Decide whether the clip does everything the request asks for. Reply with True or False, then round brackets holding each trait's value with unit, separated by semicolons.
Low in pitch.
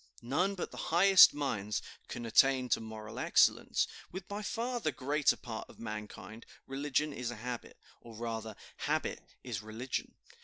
True (125 Hz)